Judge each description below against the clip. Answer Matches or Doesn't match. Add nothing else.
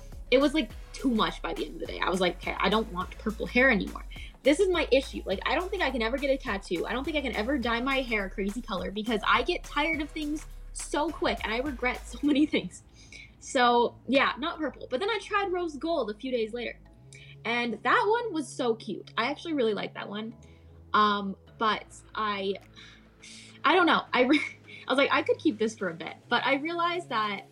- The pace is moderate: Doesn't match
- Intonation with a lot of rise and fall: Matches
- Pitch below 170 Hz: Doesn't match